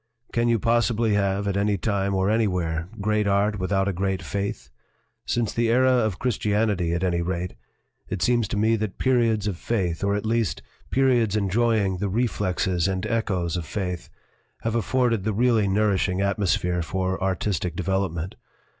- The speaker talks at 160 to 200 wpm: Yes, average, 165 wpm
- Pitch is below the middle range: Yes, low, 100 Hz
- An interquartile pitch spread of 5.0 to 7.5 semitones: No, average, 3.2 semitones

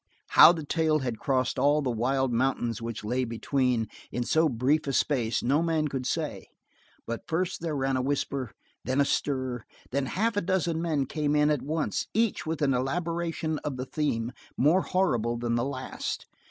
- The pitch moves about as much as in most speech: Yes, average, 4.1 semitones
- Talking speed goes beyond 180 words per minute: Yes, average, 195 wpm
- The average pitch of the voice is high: No, medium, 140 Hz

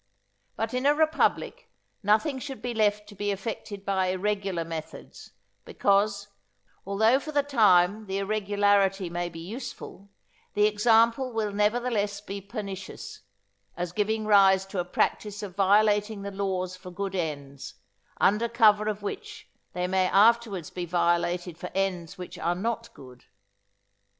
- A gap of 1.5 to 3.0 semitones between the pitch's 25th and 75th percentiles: Yes, average, 2.7 semitones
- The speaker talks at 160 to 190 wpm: No, average, 145 wpm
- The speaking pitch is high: Yes, high, 200 Hz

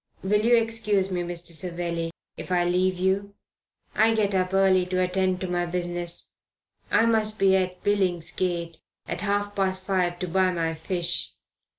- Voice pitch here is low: No, medium, 185 Hz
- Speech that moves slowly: No, average, 165 wpm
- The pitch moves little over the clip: Yes, narrow, 2.1 semitones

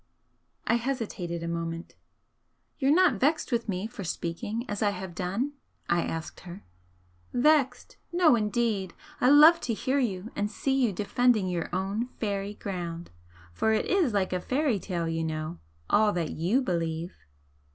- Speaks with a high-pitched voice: Yes, high, 205 Hz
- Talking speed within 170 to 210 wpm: No, average, 160 wpm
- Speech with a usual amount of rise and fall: No, wide, 6.0 semitones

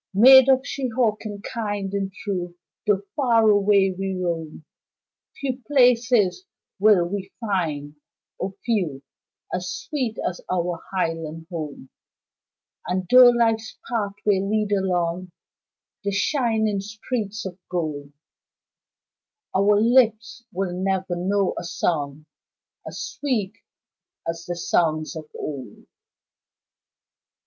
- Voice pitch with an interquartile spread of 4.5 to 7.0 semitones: No, average, 3.9 semitones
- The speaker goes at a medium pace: No, slow, 105 wpm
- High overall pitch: Yes, high, 195 Hz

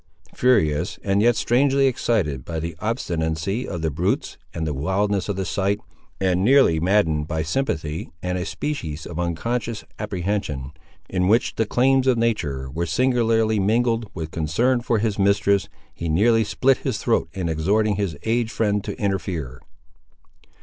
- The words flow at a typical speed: Yes, average, 155 wpm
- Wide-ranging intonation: Yes, wide, 5.8 semitones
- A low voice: Yes, low, 100 Hz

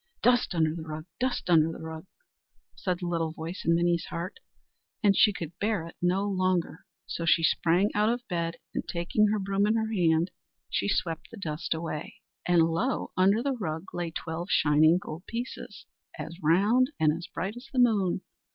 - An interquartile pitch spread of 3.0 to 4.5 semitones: Yes, average, 4.0 semitones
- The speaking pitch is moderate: Yes, medium, 175 Hz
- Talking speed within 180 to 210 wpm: Yes, average, 190 wpm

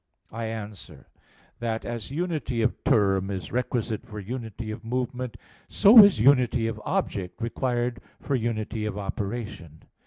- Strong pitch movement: No, average, 2.7 semitones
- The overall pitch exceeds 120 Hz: No, low, 115 Hz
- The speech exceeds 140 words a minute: No, slow, 135 wpm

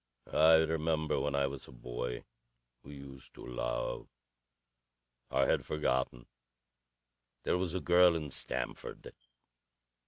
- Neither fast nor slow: No, slow, 120 wpm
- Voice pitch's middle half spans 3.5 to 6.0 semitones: Yes, average, 3.8 semitones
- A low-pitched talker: Yes, very low, 70 Hz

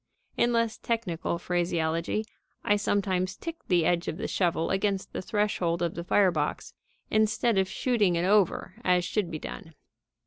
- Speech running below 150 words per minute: No, average, 165 wpm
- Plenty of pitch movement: No, average, 3.5 semitones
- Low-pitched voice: No, medium, 185 Hz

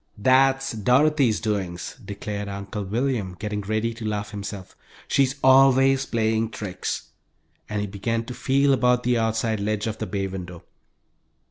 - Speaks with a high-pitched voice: No, low, 110 Hz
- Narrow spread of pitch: No, average, 3.7 semitones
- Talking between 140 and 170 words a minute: Yes, average, 145 wpm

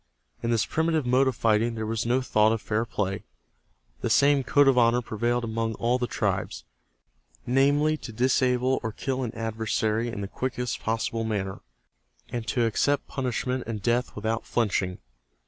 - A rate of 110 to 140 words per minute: No, average, 165 wpm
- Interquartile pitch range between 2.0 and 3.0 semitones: Yes, narrow, 2.4 semitones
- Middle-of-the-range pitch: No, low, 120 Hz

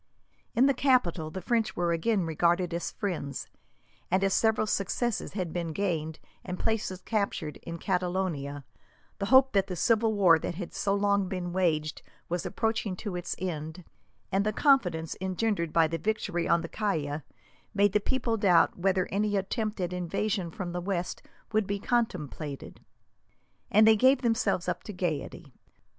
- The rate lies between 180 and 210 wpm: No, average, 160 wpm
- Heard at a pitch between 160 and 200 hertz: Yes, medium, 185 Hz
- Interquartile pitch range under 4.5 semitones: Yes, average, 4.0 semitones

